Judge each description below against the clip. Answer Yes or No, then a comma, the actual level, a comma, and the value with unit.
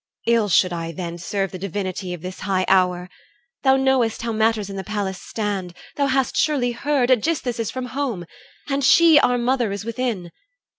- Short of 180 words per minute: No, average, 185 wpm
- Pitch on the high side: Yes, high, 220 Hz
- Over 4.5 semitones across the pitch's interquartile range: Yes, wide, 5.4 semitones